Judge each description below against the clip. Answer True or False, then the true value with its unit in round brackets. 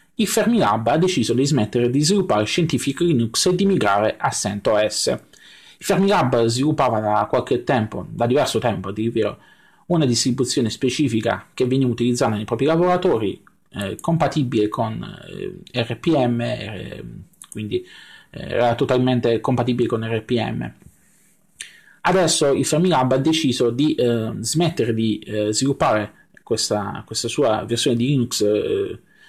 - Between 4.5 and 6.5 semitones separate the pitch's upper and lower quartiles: True (5.2 semitones)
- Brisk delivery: False (130 wpm)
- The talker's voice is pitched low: True (125 Hz)